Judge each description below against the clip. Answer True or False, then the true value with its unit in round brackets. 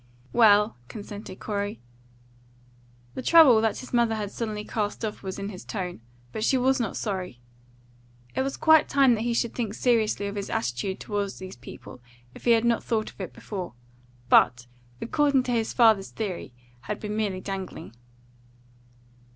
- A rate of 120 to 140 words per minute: False (165 wpm)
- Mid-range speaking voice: False (215 Hz)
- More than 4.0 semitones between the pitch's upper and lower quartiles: False (3.3 semitones)